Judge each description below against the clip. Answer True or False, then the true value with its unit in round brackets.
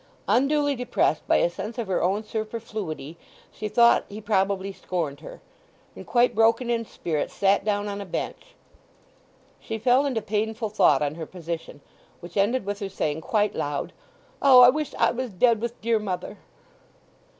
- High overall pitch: True (210 Hz)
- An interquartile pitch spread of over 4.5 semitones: False (4.1 semitones)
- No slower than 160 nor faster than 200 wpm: True (170 wpm)